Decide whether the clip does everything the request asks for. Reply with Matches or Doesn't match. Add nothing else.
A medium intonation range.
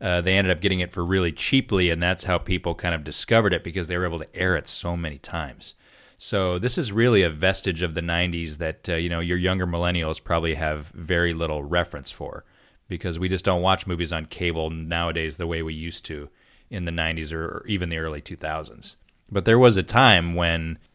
Doesn't match